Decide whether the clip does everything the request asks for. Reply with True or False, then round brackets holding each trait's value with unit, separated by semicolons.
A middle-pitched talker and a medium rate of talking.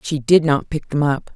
False (150 Hz; 265 wpm)